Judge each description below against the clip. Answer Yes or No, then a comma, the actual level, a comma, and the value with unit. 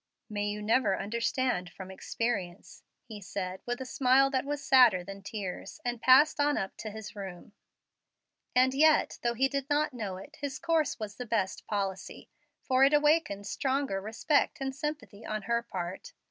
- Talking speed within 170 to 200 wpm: Yes, average, 175 wpm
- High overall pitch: Yes, high, 235 Hz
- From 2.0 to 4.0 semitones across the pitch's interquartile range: No, wide, 5.4 semitones